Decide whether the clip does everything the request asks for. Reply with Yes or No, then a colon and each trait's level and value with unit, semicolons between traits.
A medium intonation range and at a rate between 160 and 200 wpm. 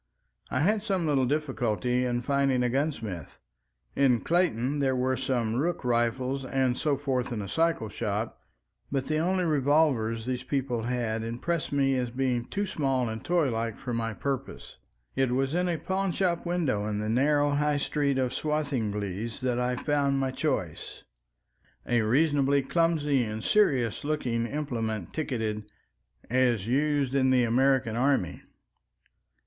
No: average, 3.9 semitones; average, 150 wpm